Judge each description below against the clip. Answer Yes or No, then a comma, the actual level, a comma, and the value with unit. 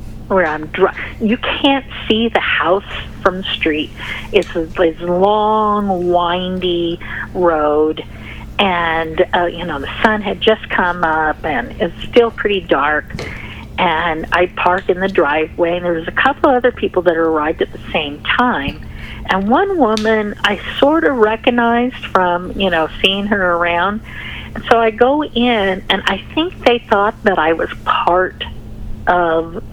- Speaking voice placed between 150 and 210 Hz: Yes, medium, 185 Hz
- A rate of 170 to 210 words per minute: No, average, 155 wpm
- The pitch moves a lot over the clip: No, average, 4.7 semitones